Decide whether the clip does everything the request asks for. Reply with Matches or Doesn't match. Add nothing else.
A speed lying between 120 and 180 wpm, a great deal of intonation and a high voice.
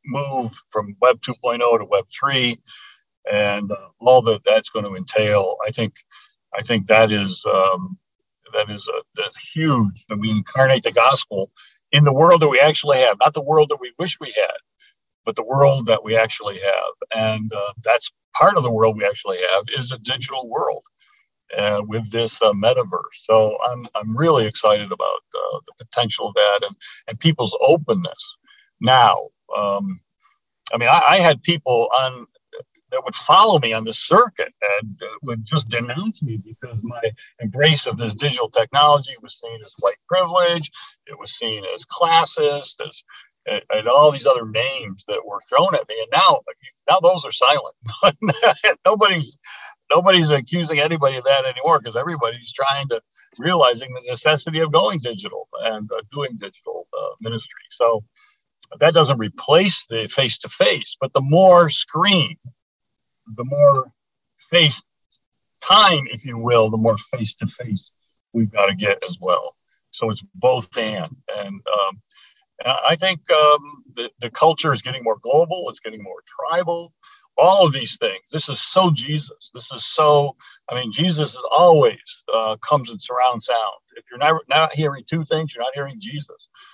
Doesn't match